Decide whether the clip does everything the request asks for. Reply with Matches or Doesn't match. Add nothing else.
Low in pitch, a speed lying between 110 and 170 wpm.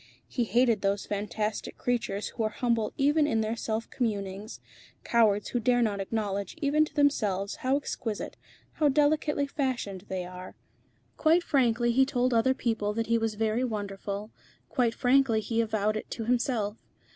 Doesn't match